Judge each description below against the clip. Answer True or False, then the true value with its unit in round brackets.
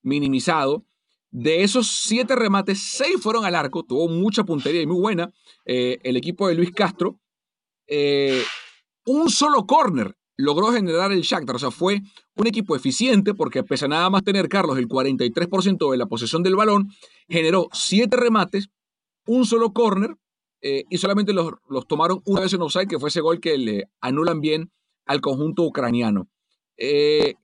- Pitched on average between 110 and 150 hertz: False (185 Hz)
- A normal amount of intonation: False (5.8 semitones)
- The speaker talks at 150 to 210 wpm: True (170 wpm)